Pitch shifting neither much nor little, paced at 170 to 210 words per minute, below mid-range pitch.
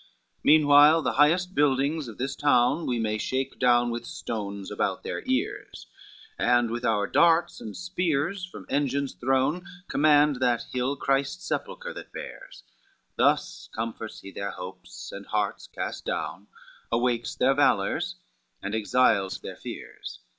No: average, 4.5 semitones; average, 145 wpm; low, 130 Hz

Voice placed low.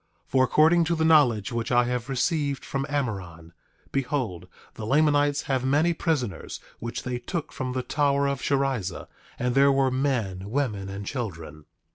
Yes: low, 130 Hz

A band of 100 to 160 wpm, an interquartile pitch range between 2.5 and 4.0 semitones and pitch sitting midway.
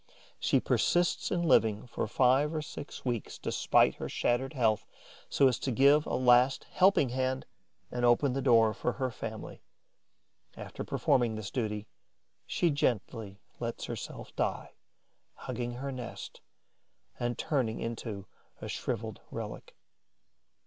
No: slow, 135 wpm; average, 3.2 semitones; low, 125 Hz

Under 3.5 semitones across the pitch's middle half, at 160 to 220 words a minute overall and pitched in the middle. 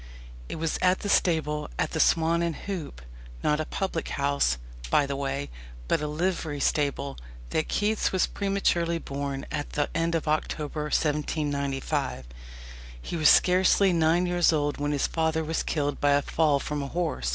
Yes: average, 2.8 semitones; average, 170 wpm; medium, 155 Hz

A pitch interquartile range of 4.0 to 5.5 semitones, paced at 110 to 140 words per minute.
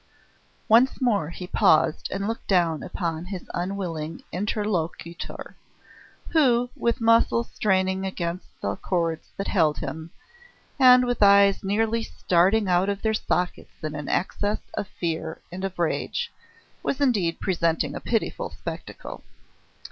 Yes: average, 4.6 semitones; slow, 135 wpm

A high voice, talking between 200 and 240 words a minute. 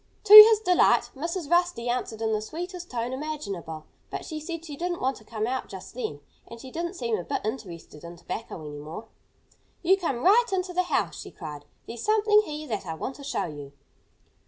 Yes: very high, 260 Hz; fast, 205 wpm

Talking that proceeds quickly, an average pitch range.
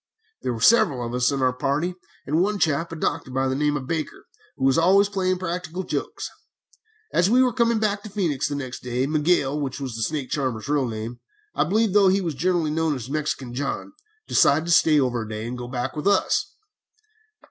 No: fast, 215 wpm; wide, 5.8 semitones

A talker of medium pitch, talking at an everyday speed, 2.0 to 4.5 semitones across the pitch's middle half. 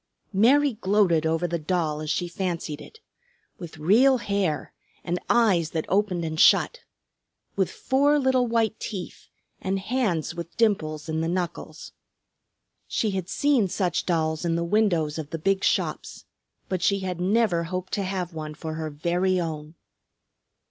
Yes: medium, 180 Hz; average, 155 wpm; average, 4.2 semitones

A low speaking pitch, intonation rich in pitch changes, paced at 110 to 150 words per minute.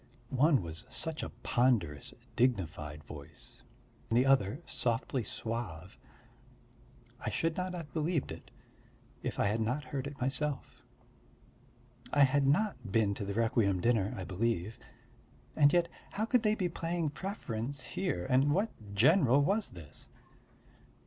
Yes: low, 130 Hz; wide, 7.1 semitones; slow, 135 wpm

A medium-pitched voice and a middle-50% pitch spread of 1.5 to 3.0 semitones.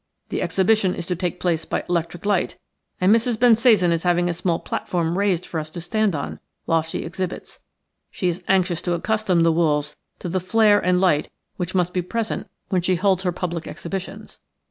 Yes: medium, 180 Hz; narrow, 2.4 semitones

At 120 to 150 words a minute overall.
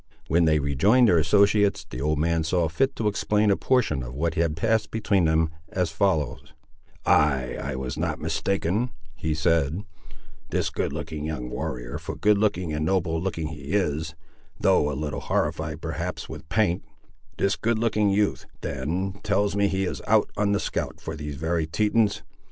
No: average, 170 wpm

